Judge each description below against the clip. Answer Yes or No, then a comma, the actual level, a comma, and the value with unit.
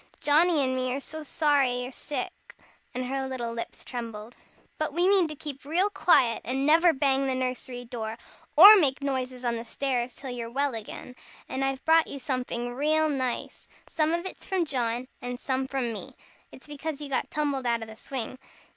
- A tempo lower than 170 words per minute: No, average, 195 wpm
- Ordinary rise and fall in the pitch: Yes, average, 3.2 semitones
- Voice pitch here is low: No, very high, 265 Hz